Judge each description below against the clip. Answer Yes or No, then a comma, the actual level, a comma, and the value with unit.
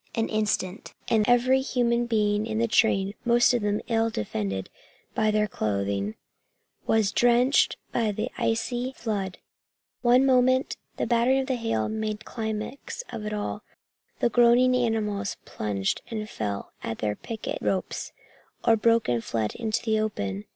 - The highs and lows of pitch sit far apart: No, average, 3.2 semitones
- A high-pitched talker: Yes, high, 220 Hz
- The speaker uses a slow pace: No, average, 150 wpm